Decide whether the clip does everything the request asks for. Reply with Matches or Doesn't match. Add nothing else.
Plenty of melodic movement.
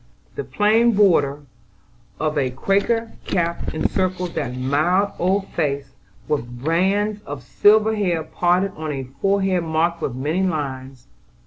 Matches